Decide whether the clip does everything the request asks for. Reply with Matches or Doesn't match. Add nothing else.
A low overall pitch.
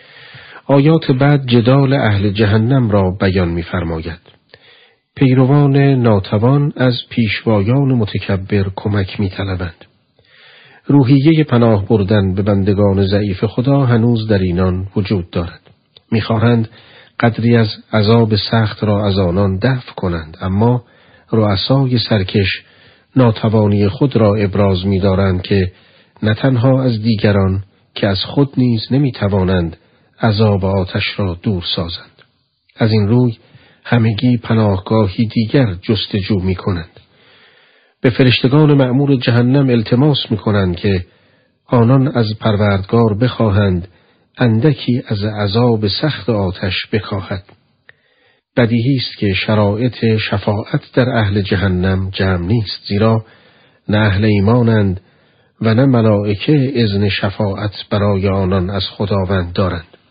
Matches